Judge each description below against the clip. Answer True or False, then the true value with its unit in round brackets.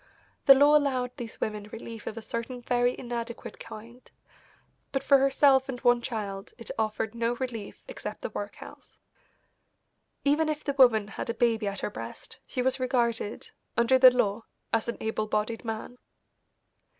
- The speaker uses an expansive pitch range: False (2.7 semitones)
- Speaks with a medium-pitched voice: False (240 Hz)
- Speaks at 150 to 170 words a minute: True (160 wpm)